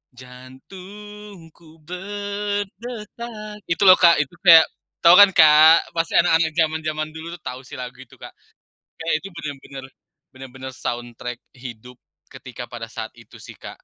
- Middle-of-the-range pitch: Yes, medium, 160 Hz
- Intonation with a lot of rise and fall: Yes, wide, 6.9 semitones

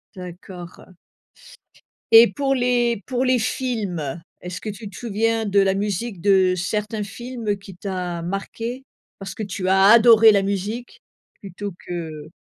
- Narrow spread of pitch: No, average, 3.7 semitones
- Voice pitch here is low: No, high, 200 Hz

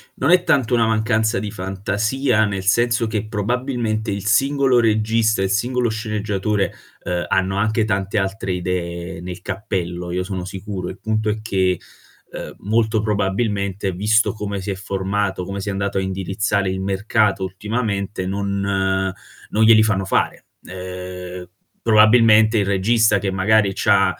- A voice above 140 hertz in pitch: No, low, 100 Hz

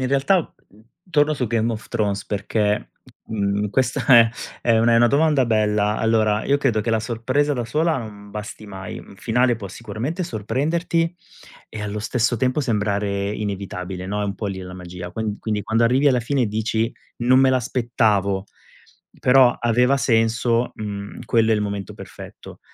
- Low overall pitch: Yes, low, 110 Hz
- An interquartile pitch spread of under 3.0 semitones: No, average, 3.5 semitones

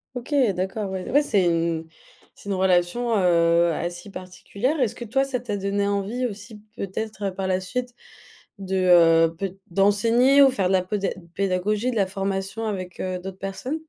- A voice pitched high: Yes, high, 195 Hz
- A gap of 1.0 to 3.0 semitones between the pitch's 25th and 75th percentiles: No, average, 3.4 semitones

